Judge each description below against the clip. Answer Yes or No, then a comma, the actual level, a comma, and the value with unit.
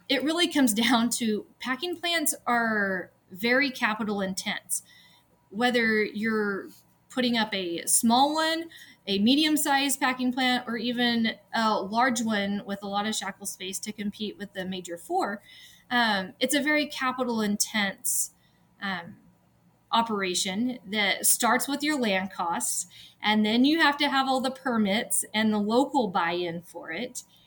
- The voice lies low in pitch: No, high, 230 Hz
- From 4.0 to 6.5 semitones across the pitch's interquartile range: Yes, average, 4.3 semitones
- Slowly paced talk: No, average, 155 wpm